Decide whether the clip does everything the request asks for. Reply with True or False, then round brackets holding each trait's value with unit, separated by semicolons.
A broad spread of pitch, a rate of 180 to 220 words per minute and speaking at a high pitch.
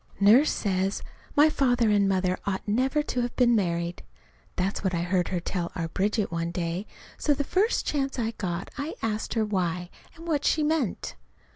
True (6.2 semitones; 185 wpm; 205 Hz)